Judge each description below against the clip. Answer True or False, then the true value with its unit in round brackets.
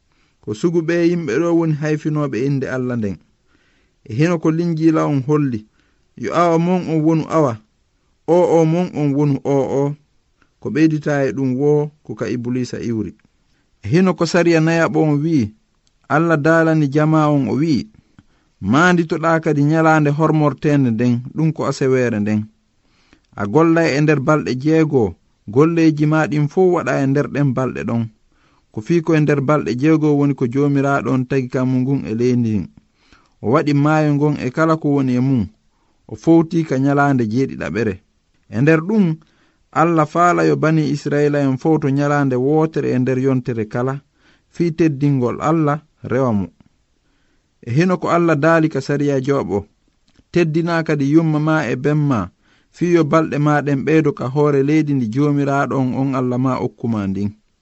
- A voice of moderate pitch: True (145 Hz)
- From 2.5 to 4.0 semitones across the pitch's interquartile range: True (3.6 semitones)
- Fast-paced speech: False (160 wpm)